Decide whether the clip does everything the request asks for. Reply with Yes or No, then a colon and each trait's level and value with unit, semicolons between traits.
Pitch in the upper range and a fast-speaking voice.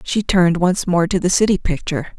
No: medium, 180 Hz; fast, 220 wpm